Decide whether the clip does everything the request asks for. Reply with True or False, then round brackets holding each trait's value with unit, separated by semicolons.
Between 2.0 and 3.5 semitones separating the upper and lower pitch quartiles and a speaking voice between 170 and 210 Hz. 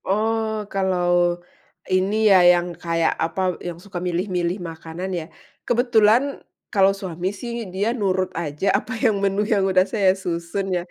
True (2.7 semitones; 190 Hz)